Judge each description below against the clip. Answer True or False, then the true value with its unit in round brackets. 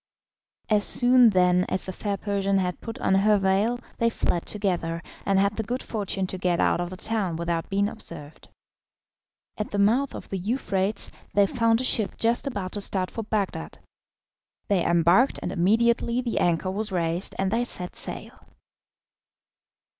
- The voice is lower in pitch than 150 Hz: False (200 Hz)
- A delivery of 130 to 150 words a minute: False (170 wpm)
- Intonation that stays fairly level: False (3.5 semitones)